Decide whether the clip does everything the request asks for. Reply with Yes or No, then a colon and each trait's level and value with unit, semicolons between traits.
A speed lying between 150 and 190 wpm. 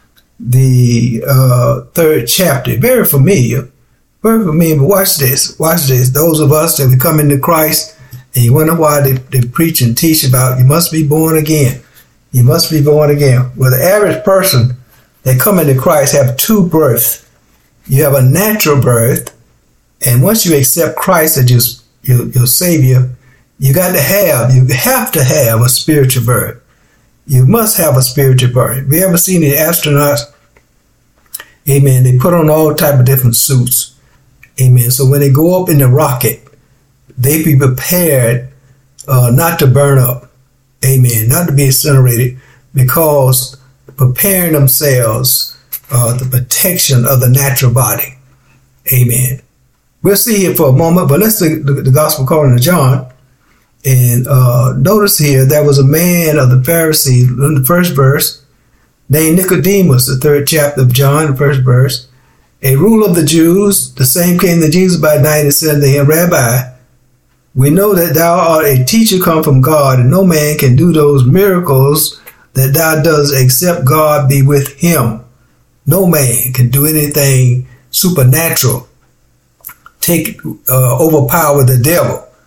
Yes: average, 165 wpm